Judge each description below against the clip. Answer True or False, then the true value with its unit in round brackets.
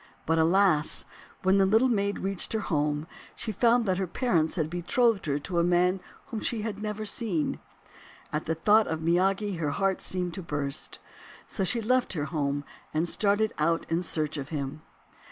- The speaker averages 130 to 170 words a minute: False (185 wpm)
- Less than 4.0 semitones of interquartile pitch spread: False (4.7 semitones)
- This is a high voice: False (180 Hz)